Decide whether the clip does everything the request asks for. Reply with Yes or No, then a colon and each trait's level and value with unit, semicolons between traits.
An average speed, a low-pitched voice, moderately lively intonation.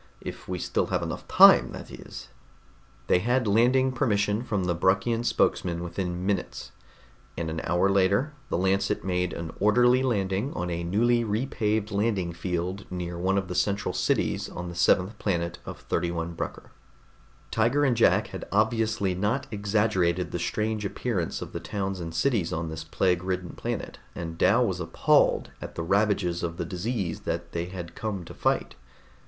Yes: average, 170 wpm; very low, 95 Hz; average, 3.8 semitones